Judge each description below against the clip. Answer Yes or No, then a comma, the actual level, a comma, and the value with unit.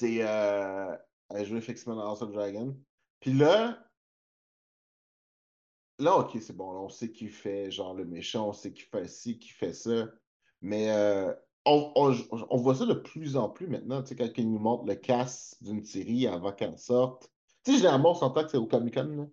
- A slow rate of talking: No, average, 195 wpm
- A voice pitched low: Yes, low, 115 Hz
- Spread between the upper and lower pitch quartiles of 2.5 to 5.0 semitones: Yes, average, 4.2 semitones